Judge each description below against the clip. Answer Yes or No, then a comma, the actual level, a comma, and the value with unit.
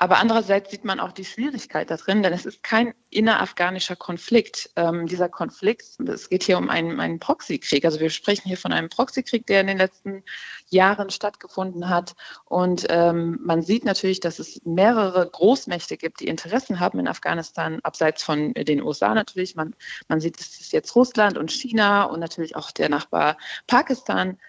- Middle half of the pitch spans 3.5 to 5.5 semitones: Yes, average, 3.9 semitones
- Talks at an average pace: Yes, average, 180 wpm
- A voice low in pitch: No, medium, 185 Hz